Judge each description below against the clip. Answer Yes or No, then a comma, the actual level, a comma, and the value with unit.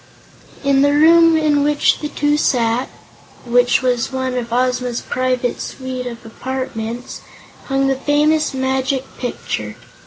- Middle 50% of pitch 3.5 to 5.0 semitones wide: No, average, 2.7 semitones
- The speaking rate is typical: No, slow, 130 wpm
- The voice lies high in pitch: Yes, very high, 260 Hz